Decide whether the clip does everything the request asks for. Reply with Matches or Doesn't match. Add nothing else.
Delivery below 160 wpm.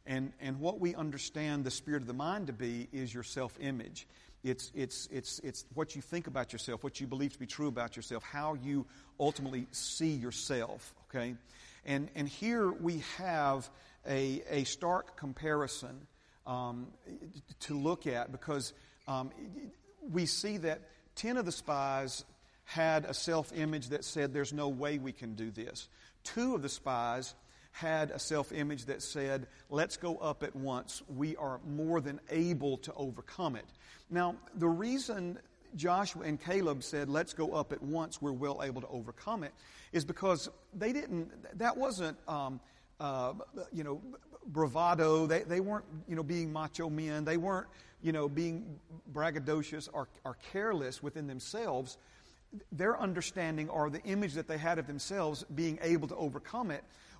Doesn't match